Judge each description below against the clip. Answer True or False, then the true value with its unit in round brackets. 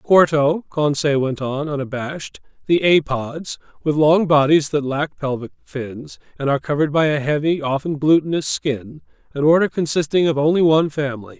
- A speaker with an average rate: True (160 wpm)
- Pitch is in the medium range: True (150 Hz)